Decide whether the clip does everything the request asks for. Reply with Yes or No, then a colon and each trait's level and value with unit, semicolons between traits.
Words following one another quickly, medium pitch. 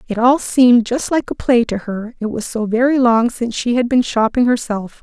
No: fast, 240 wpm; high, 235 Hz